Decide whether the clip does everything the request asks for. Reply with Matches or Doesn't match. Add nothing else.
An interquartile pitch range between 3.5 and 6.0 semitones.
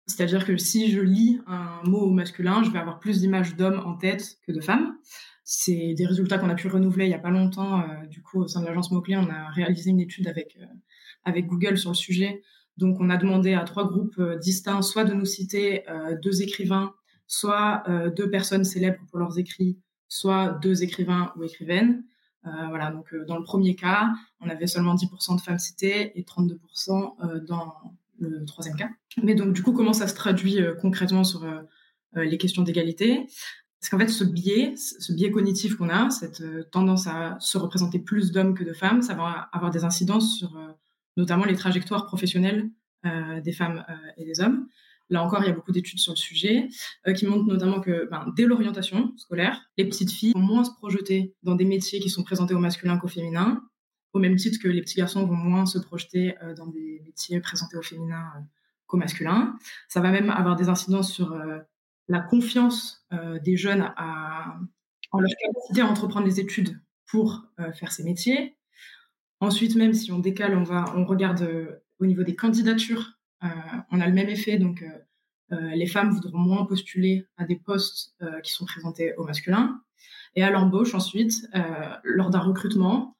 Doesn't match